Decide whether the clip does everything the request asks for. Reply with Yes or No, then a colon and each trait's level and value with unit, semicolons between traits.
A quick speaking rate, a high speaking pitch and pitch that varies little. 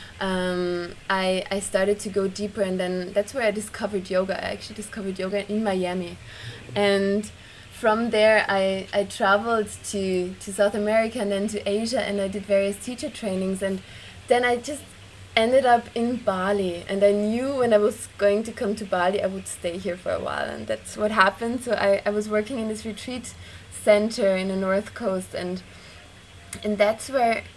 No: average, 190 wpm; high, 200 Hz; narrow, 2.1 semitones